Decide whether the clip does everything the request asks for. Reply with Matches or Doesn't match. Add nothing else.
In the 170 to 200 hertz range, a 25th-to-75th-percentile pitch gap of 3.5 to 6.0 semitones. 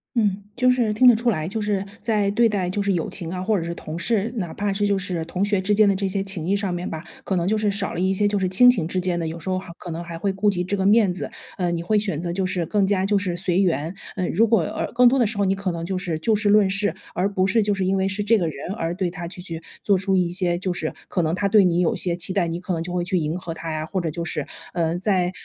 Doesn't match